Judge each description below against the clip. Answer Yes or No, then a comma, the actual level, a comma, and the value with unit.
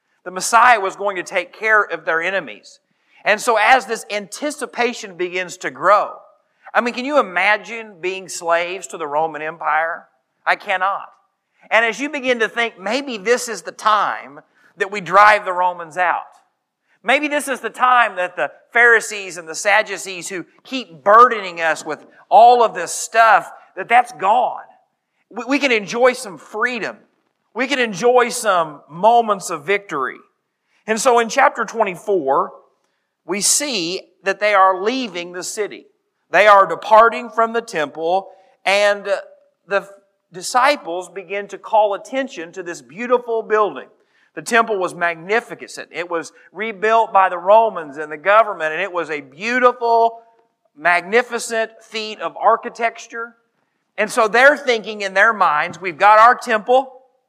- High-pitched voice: Yes, high, 215 Hz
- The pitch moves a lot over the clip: No, average, 4.5 semitones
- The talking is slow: No, average, 155 wpm